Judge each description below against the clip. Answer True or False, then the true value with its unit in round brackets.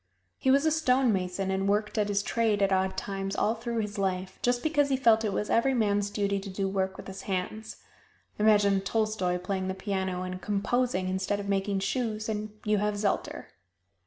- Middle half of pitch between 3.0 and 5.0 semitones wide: False (2.4 semitones)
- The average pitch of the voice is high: True (205 Hz)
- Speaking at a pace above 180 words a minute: True (195 wpm)